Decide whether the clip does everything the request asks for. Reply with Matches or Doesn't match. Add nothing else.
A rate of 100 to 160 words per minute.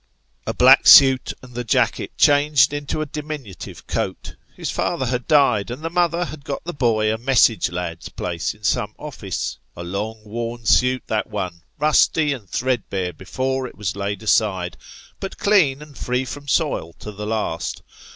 Doesn't match